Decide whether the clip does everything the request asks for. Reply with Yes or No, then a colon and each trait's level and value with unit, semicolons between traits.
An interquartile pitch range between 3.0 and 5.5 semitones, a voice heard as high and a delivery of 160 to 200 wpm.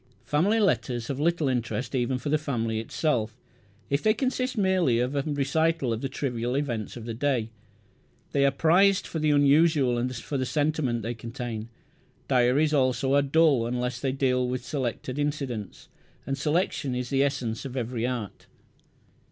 No: average, 3.5 semitones; low, 135 Hz; average, 170 wpm